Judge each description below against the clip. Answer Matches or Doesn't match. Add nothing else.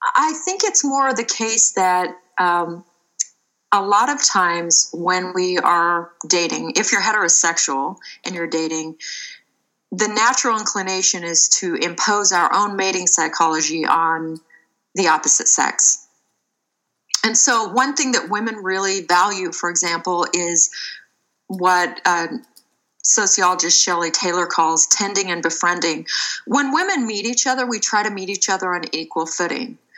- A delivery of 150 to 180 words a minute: Doesn't match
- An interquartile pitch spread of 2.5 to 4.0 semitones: Doesn't match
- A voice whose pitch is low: Doesn't match